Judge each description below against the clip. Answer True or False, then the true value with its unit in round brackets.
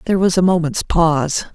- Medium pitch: True (175 Hz)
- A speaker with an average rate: True (195 wpm)